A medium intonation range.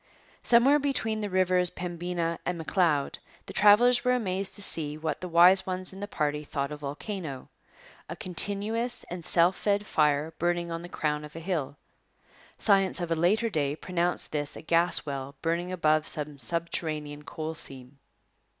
Yes: average, 4.1 semitones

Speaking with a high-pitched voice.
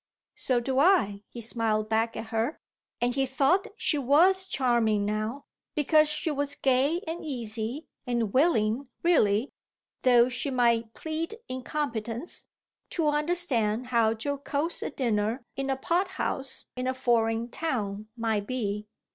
Yes: very high, 255 Hz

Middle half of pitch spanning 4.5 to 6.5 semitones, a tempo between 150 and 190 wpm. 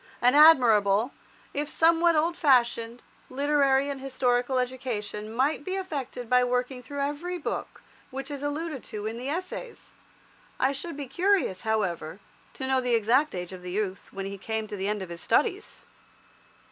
Yes: average, 4.9 semitones; average, 170 wpm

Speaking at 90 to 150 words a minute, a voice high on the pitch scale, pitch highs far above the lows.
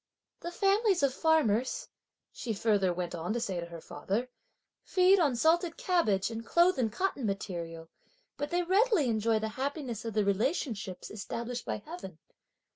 No: average, 160 wpm; high, 235 Hz; wide, 8.7 semitones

